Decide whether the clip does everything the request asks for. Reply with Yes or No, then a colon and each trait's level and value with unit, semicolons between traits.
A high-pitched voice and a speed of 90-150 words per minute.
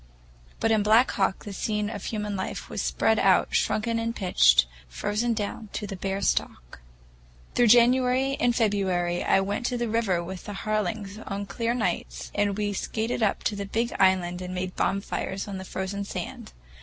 No: high, 205 Hz; average, 180 wpm